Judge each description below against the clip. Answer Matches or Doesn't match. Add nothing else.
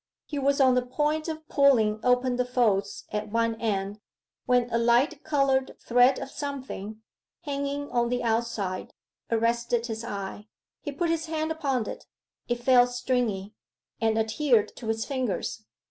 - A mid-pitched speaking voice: Doesn't match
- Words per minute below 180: Matches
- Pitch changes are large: Doesn't match